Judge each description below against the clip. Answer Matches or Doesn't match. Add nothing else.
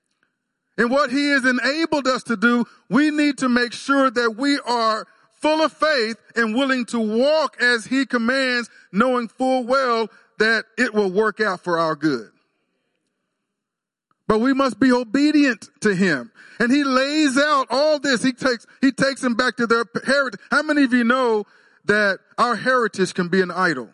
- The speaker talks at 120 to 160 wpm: Doesn't match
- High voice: Matches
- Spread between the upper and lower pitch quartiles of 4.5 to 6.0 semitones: Doesn't match